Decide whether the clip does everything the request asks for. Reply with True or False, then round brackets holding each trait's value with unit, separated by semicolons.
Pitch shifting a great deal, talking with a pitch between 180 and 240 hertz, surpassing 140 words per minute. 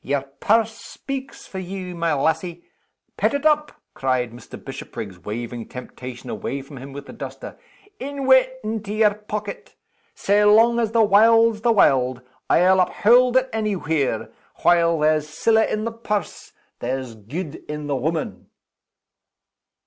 True (8.2 semitones; 185 Hz; 150 wpm)